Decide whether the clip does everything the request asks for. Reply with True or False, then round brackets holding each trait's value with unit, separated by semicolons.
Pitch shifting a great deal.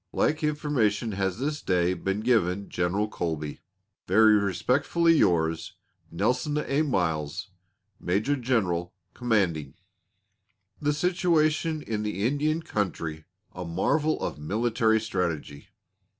True (8.4 semitones)